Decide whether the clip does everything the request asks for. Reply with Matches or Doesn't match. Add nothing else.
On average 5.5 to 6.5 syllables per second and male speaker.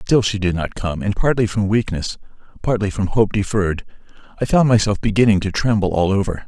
Matches